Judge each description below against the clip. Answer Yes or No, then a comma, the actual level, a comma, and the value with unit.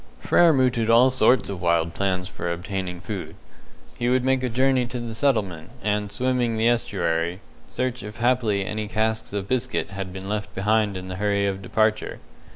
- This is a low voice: Yes, low, 105 Hz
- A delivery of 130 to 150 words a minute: No, average, 180 wpm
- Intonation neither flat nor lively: Yes, average, 4.1 semitones